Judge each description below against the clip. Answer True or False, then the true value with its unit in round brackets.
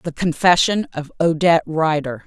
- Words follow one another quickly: False (130 wpm)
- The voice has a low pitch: False (160 Hz)